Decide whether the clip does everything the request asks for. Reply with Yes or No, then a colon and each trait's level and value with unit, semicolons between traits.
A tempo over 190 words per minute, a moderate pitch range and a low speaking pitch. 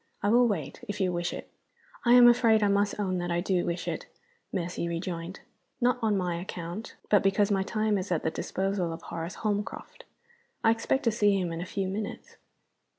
No: fast, 205 wpm; average, 3.5 semitones; high, 195 Hz